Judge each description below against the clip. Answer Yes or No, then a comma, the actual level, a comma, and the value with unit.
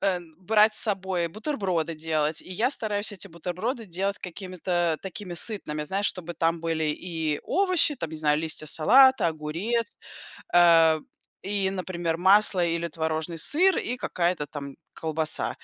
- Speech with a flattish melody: No, average, 4.1 semitones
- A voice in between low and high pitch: Yes, medium, 175 Hz